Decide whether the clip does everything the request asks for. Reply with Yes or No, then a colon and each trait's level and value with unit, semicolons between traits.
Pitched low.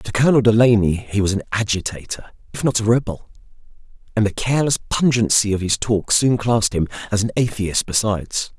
Yes: low, 110 Hz